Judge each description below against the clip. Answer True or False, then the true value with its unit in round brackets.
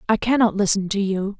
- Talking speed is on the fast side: True (215 wpm)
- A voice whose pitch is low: False (205 Hz)